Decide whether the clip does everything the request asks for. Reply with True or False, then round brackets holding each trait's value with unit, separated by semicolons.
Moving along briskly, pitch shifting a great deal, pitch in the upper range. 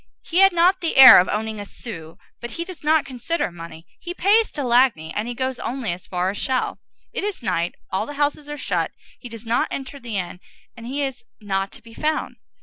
True (230 wpm; 6.5 semitones; 245 Hz)